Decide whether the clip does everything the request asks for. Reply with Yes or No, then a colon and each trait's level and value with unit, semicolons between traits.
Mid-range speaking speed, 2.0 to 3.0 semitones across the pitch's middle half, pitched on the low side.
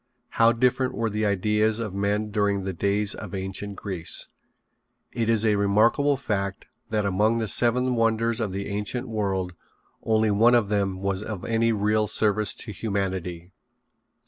Yes: average, 160 wpm; narrow, 2.4 semitones; low, 105 Hz